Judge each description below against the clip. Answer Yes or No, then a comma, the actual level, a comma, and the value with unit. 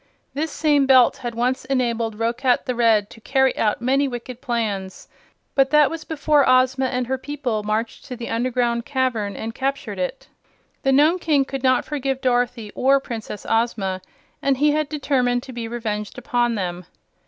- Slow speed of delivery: No, average, 175 wpm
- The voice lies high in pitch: Yes, very high, 250 Hz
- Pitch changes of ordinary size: Yes, average, 3.0 semitones